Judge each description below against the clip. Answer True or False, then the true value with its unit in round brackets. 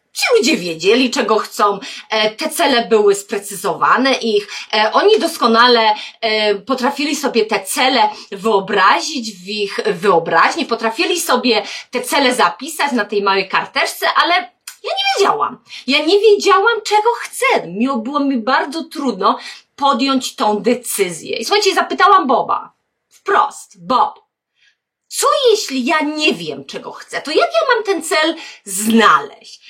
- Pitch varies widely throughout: True (7.3 semitones)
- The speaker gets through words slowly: False (130 wpm)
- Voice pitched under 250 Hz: False (255 Hz)